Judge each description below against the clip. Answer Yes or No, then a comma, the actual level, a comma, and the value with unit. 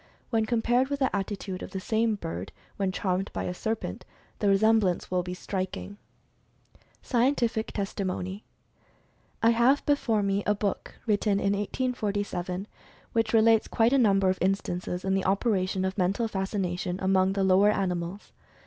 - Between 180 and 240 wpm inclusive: No, average, 155 wpm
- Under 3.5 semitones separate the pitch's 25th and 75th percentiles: Yes, average, 3.0 semitones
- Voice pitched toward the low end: No, high, 200 Hz